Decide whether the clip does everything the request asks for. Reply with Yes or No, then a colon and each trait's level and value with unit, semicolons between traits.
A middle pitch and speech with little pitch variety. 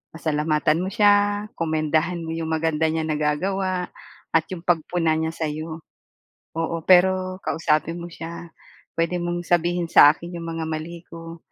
Yes: medium, 165 Hz; narrow, 1.8 semitones